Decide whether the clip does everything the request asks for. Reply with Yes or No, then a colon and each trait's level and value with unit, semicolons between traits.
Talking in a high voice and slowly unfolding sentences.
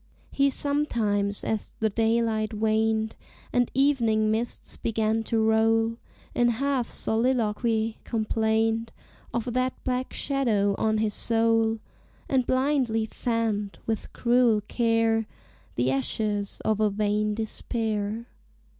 Yes: high, 225 Hz; slow, 110 wpm